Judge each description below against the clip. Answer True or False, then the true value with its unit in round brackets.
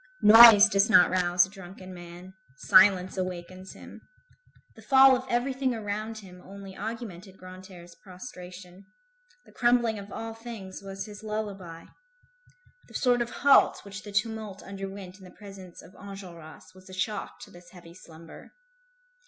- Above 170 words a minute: False (150 wpm)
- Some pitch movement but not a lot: True (3.0 semitones)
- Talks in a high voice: True (195 Hz)